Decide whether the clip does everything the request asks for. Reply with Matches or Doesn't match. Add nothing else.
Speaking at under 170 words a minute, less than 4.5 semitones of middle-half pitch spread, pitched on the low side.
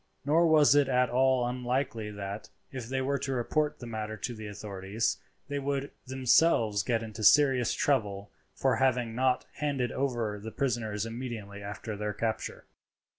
Matches